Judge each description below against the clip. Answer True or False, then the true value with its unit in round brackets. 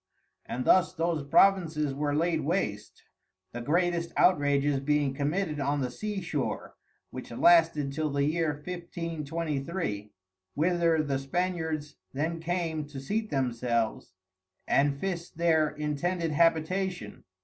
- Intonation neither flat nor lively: True (3.4 semitones)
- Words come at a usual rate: False (120 wpm)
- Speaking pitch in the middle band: True (155 Hz)